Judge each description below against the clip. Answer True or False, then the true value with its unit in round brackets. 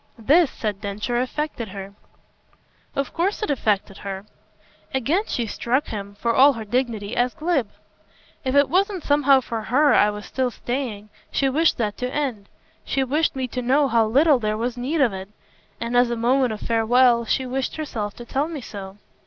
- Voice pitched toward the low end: False (245 Hz)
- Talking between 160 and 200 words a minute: True (185 wpm)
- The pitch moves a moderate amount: True (4.3 semitones)